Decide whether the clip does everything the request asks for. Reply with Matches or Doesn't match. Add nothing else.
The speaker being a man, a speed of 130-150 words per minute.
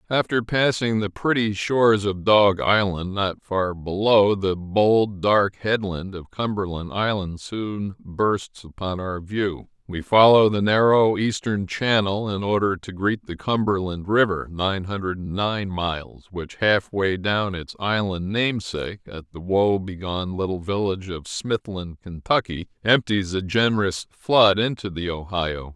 Matches